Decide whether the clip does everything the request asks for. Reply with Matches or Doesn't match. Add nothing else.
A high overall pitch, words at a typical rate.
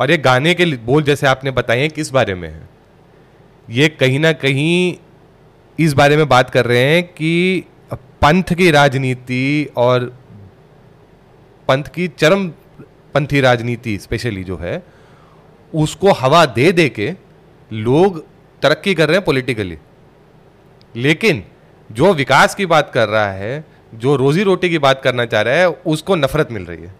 Doesn't match